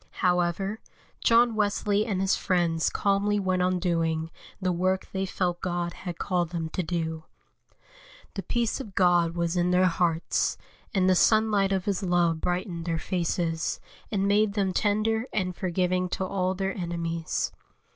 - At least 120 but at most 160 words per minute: Yes, average, 155 wpm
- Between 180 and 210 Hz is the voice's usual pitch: Yes, medium, 185 Hz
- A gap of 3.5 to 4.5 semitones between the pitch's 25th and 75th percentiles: No, narrow, 2.4 semitones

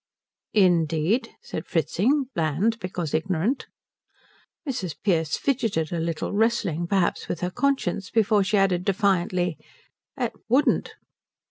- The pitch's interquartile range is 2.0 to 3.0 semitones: No, average, 4.8 semitones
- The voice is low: No, medium, 185 Hz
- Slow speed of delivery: Yes, slow, 115 wpm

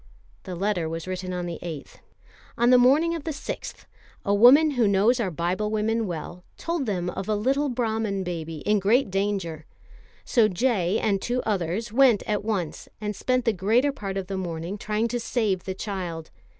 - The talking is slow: No, average, 185 wpm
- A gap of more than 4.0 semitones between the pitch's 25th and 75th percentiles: Yes, average, 4.6 semitones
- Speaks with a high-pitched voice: Yes, high, 205 Hz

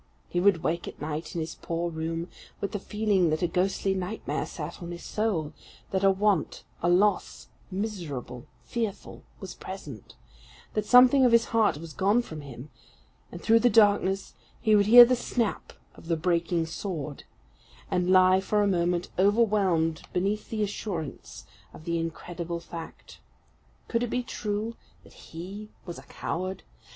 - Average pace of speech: Yes, average, 165 wpm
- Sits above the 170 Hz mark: Yes, medium, 185 Hz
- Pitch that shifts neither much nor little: Yes, average, 4.0 semitones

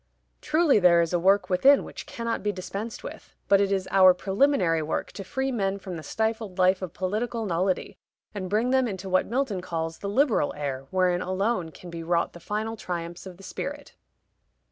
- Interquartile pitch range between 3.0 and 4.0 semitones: Yes, average, 3.7 semitones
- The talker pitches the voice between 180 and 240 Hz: Yes, high, 190 Hz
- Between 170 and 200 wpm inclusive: Yes, average, 195 wpm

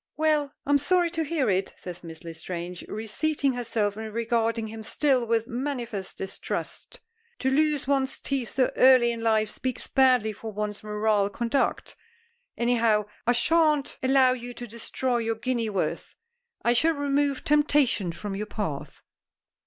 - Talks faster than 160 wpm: No, average, 150 wpm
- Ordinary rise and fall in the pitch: Yes, average, 4.2 semitones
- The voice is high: Yes, high, 235 Hz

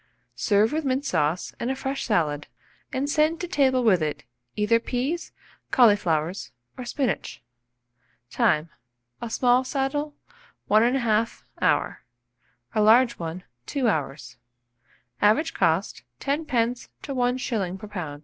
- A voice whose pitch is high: Yes, high, 235 Hz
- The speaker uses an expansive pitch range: Yes, wide, 6.5 semitones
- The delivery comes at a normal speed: No, slow, 125 wpm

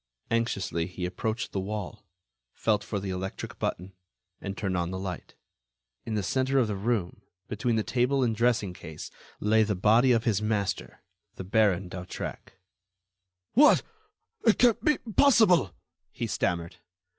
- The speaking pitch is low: Yes, low, 105 Hz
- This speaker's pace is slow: No, average, 150 wpm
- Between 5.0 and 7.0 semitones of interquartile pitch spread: No, average, 4.3 semitones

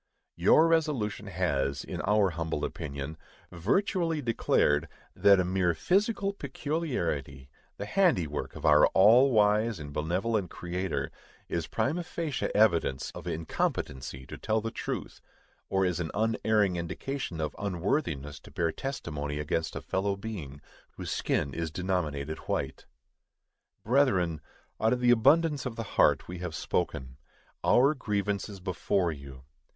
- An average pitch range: No, wide, 6.7 semitones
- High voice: No, very low, 95 Hz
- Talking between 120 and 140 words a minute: Yes, slow, 135 wpm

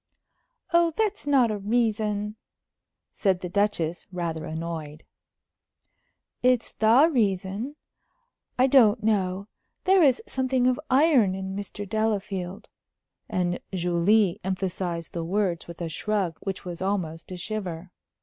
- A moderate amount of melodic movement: Yes, average, 4.1 semitones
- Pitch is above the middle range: Yes, high, 200 Hz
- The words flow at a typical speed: No, slow, 120 wpm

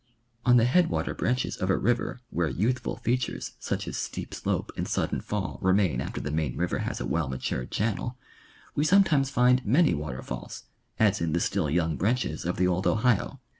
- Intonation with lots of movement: Yes, wide, 7.2 semitones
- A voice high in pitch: No, low, 105 Hz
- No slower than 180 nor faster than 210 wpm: Yes, average, 190 wpm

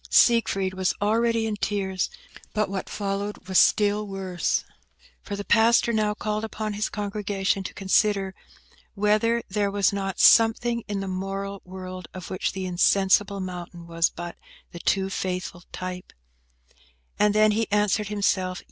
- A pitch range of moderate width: No, narrow, 2.1 semitones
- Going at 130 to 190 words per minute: Yes, average, 145 wpm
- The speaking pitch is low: No, high, 200 Hz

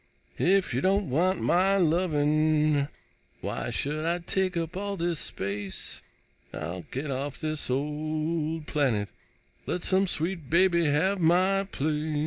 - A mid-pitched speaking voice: Yes, medium, 155 Hz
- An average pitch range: Yes, average, 3.8 semitones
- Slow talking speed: Yes, slow, 130 wpm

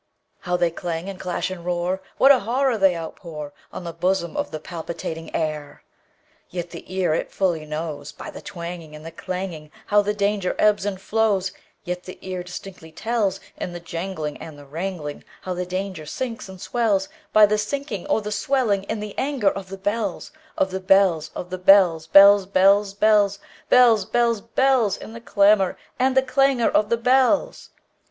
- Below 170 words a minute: Yes, average, 155 wpm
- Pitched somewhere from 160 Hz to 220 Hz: Yes, high, 190 Hz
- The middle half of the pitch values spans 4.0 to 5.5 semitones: No, average, 3.5 semitones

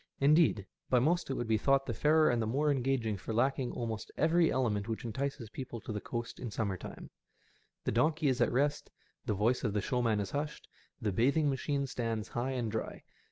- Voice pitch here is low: Yes, low, 125 Hz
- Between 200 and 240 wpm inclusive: Yes, fast, 205 wpm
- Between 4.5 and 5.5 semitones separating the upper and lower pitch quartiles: No, average, 3.9 semitones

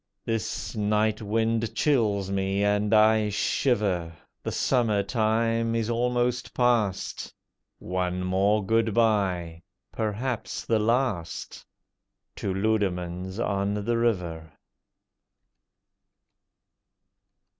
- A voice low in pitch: Yes, low, 105 Hz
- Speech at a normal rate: No, slow, 85 wpm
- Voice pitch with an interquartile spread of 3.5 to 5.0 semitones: No, average, 2.9 semitones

